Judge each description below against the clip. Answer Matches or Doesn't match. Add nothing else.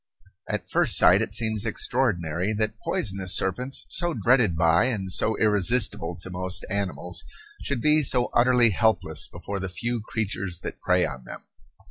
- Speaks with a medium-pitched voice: Doesn't match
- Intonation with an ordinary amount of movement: Matches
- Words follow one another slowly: Doesn't match